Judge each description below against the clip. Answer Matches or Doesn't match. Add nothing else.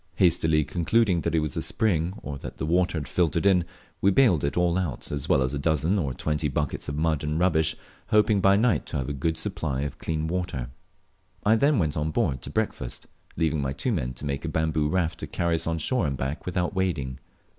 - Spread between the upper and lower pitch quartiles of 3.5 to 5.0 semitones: Matches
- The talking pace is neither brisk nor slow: Doesn't match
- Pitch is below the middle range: Matches